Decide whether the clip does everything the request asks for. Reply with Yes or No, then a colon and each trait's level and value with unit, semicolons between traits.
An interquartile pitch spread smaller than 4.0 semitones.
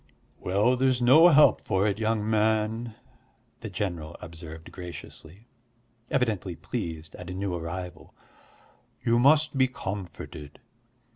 No: wide, 5.4 semitones